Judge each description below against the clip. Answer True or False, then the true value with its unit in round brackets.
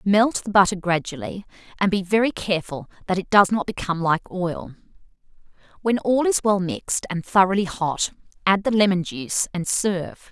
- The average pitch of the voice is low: False (190 Hz)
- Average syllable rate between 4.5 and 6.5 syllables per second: True (5.3 syllables/s)